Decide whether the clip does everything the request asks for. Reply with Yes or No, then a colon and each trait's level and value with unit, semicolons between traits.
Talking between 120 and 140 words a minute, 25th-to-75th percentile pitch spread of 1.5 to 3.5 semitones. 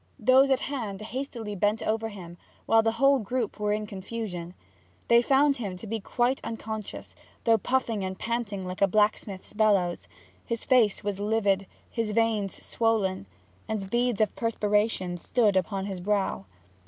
No: average, 155 wpm; average, 2.8 semitones